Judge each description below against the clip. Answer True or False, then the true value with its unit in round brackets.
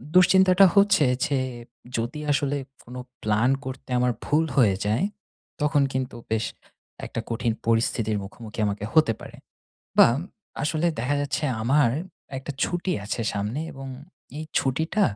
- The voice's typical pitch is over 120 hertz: True (130 Hz)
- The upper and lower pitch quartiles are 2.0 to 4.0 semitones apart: False (5.2 semitones)